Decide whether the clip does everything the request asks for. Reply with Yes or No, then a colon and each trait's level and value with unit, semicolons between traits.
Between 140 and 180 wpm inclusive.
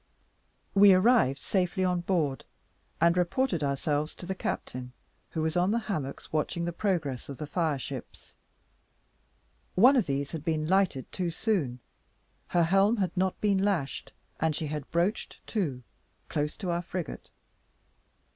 Yes: average, 150 wpm